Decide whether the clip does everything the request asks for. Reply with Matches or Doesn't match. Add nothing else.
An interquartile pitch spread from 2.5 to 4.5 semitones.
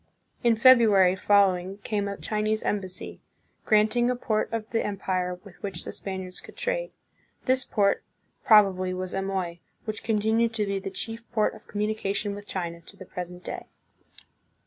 Matches